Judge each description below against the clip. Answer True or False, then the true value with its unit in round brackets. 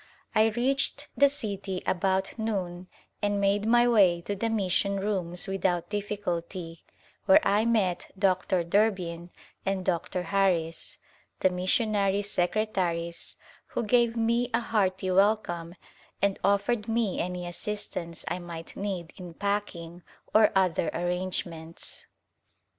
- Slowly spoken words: True (120 wpm)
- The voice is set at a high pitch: True (195 Hz)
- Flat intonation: False (3.1 semitones)